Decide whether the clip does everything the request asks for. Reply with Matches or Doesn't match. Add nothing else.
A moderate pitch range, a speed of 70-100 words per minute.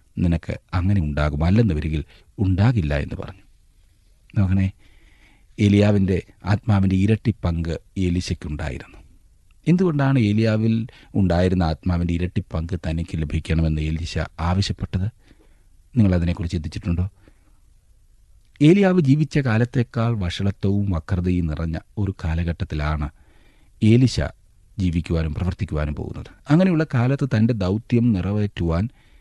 Matches